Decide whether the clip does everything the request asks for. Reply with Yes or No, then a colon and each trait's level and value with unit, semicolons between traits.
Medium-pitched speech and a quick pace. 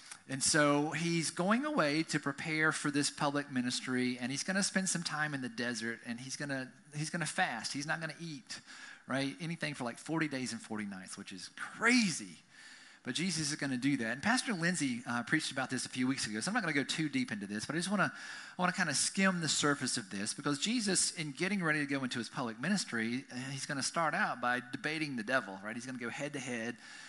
Yes: medium, 145 Hz; fast, 255 wpm